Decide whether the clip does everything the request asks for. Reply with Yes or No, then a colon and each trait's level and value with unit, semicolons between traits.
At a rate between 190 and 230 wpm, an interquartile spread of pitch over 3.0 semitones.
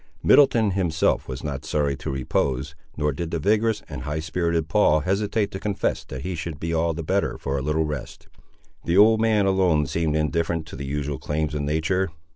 Yes: average, 200 wpm; average, 4.5 semitones